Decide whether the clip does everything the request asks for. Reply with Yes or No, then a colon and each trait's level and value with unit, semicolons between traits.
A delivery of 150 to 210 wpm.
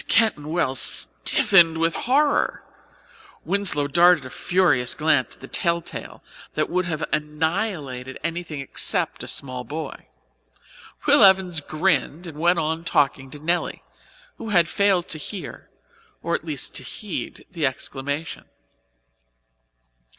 No: slow, 135 wpm